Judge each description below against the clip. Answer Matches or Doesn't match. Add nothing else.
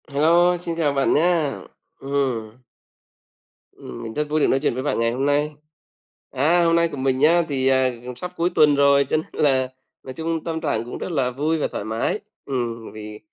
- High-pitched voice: Doesn't match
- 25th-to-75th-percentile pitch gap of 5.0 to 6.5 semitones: Doesn't match